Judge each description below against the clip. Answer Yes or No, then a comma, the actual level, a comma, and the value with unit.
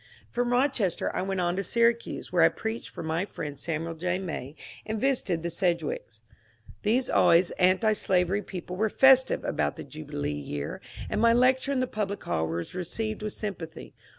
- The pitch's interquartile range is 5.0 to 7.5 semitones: Yes, wide, 5.6 semitones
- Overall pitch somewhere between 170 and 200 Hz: Yes, high, 190 Hz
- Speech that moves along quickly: No, average, 180 wpm